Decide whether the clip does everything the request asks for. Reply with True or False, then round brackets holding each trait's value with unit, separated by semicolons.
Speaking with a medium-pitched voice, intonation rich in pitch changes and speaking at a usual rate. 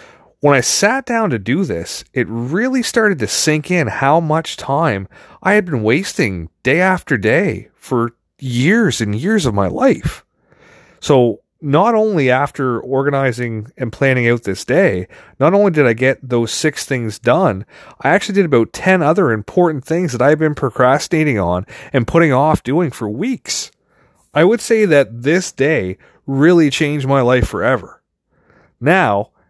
True (145 Hz; 6.5 semitones; 165 wpm)